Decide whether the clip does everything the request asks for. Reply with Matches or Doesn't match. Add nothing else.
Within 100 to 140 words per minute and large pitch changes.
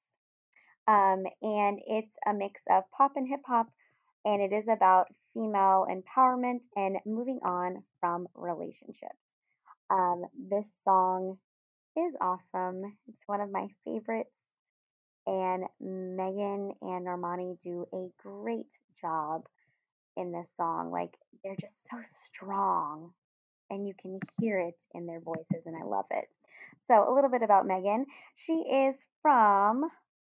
Doesn't match